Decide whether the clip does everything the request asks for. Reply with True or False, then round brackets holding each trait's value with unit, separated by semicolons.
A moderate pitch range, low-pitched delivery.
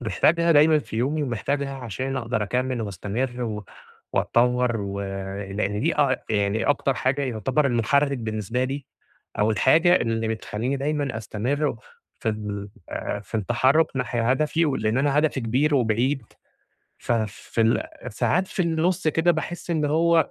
True (4.8 semitones; 130 Hz)